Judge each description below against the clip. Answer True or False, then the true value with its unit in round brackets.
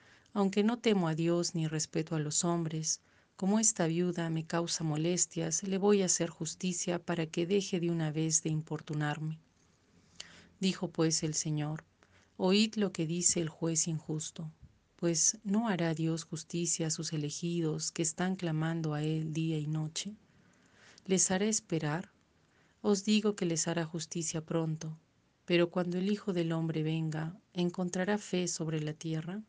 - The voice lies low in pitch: False (165 Hz)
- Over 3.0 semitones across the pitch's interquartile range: False (2.5 semitones)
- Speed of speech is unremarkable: True (160 wpm)